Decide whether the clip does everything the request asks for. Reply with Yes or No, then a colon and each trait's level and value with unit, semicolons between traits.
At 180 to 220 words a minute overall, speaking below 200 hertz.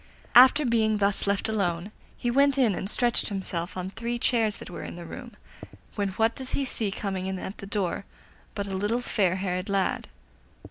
No: average, 195 wpm; high, 205 Hz